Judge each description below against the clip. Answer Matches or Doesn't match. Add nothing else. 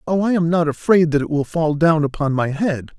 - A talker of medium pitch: Matches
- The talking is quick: Matches